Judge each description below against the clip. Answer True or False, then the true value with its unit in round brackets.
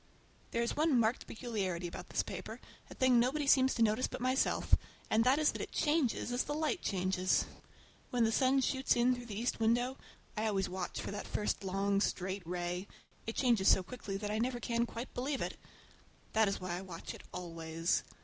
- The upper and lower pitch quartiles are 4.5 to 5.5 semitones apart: True (4.8 semitones)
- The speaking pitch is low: False (225 Hz)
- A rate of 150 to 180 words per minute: False (195 wpm)